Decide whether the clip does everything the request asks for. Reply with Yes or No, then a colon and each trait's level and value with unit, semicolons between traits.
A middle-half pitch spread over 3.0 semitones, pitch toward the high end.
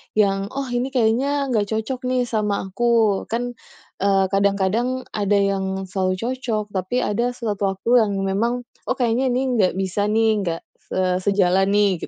Yes: average, 3.8 semitones; high, 210 Hz